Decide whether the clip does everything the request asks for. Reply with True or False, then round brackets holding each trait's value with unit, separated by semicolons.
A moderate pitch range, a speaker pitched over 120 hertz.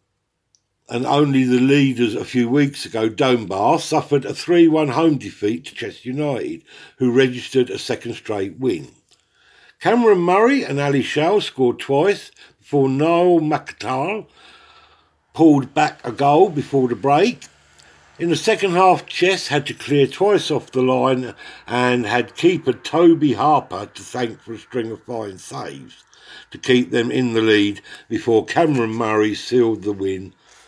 True (4.7 semitones; 135 Hz)